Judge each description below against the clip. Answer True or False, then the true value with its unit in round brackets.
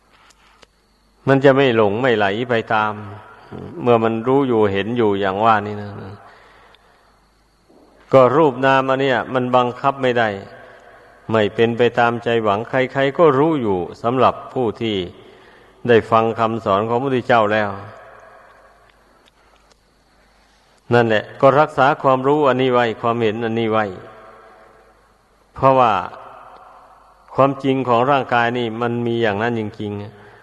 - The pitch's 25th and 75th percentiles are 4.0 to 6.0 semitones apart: False (3.2 semitones)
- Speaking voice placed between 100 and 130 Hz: True (115 Hz)